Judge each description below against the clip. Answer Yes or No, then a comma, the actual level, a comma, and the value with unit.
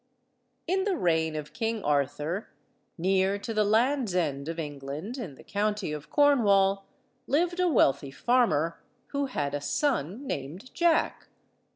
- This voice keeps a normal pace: Yes, average, 150 wpm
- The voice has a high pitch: Yes, high, 195 Hz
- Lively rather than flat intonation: Yes, wide, 8.9 semitones